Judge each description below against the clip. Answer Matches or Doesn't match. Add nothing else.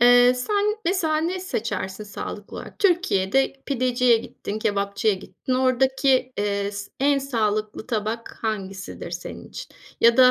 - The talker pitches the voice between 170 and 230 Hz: Doesn't match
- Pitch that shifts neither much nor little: Matches